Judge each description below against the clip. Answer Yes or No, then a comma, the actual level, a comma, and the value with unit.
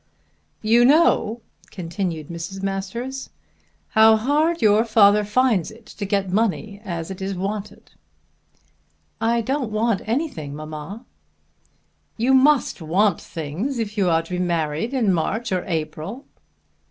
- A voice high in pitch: Yes, high, 210 Hz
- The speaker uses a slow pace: Yes, slow, 130 wpm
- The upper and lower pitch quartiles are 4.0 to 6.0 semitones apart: Yes, average, 4.7 semitones